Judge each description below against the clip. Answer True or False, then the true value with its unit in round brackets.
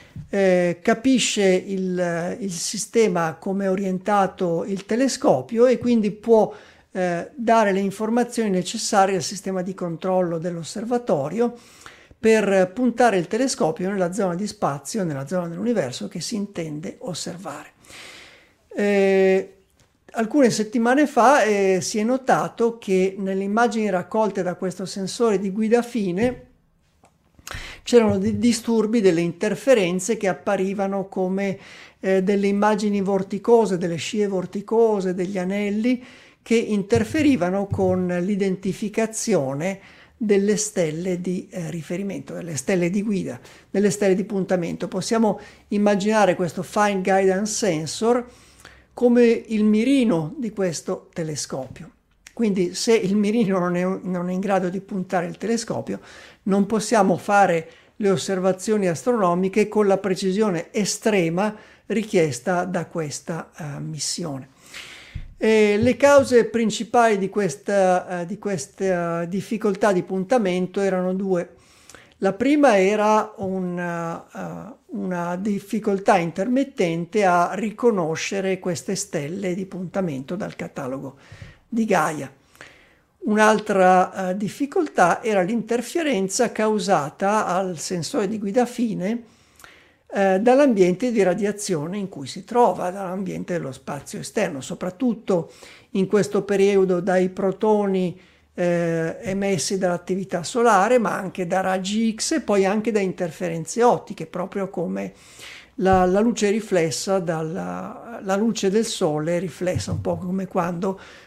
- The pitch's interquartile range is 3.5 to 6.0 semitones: False (3.1 semitones)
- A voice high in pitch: True (195 Hz)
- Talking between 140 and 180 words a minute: False (120 wpm)